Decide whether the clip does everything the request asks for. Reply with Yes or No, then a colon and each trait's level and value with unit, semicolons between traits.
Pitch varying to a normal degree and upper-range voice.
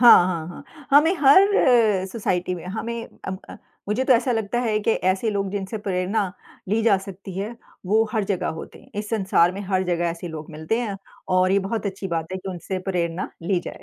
Yes: average, 3.5 semitones; high, 195 Hz